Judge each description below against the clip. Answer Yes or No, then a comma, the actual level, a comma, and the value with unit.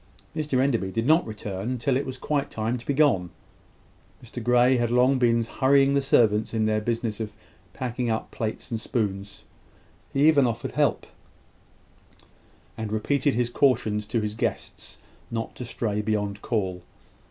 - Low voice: Yes, low, 115 Hz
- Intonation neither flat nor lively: Yes, average, 3.3 semitones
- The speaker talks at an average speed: Yes, average, 160 wpm